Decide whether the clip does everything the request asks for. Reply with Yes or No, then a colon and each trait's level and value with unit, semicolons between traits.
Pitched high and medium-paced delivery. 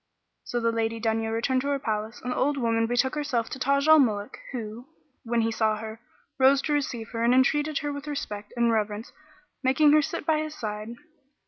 No: high, 240 Hz; fast, 210 wpm